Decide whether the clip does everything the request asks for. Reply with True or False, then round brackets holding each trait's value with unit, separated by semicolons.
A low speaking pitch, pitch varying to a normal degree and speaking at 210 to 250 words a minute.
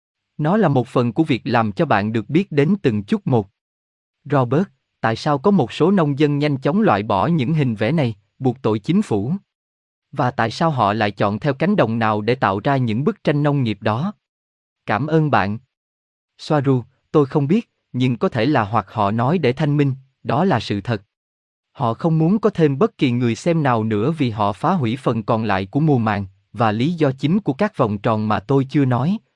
False (125 Hz; 5.9 semitones; 220 wpm)